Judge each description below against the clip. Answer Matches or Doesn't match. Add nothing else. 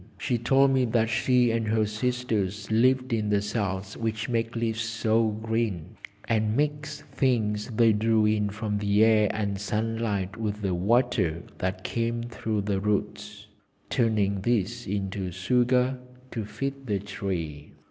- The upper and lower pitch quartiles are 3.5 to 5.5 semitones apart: Doesn't match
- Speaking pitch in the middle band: Doesn't match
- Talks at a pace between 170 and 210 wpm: Doesn't match